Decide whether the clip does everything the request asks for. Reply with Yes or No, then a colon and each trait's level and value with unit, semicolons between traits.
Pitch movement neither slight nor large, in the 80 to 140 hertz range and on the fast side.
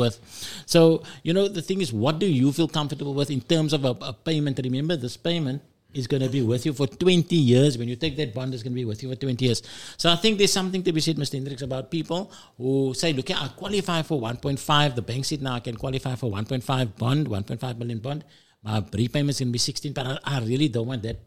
Yes: average, 4.2 semitones; low, 135 Hz; fast, 255 wpm